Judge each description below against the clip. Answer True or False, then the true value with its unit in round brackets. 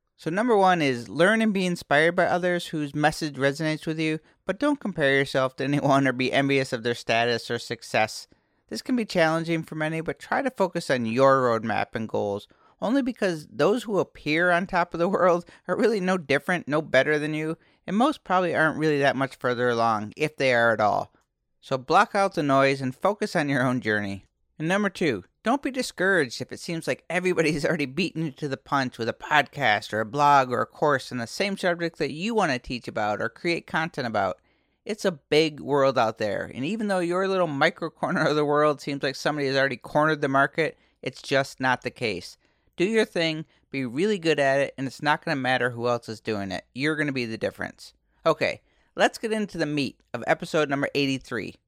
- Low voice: False (150 Hz)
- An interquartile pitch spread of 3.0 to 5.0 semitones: True (4.7 semitones)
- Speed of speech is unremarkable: False (220 wpm)